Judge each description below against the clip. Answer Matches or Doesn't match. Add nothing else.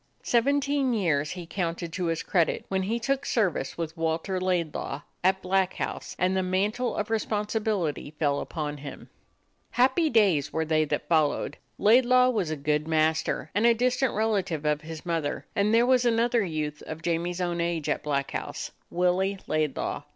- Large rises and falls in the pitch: Matches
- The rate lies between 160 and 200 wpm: Matches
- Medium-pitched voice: Matches